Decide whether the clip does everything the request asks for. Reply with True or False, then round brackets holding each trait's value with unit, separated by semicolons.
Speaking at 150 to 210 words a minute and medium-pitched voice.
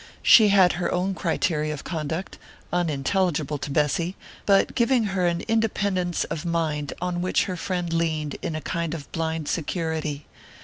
True (160 wpm; 170 Hz)